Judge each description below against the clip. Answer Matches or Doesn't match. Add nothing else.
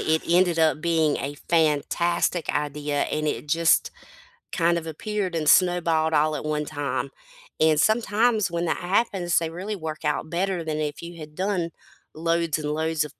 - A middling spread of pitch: Doesn't match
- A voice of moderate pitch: Matches